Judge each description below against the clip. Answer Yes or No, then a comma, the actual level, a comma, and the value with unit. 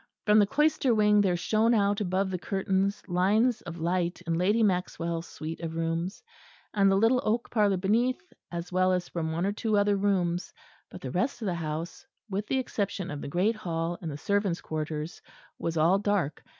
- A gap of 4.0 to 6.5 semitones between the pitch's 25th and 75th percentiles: No, average, 3.6 semitones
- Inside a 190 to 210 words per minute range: Yes, average, 195 wpm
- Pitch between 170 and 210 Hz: Yes, high, 190 Hz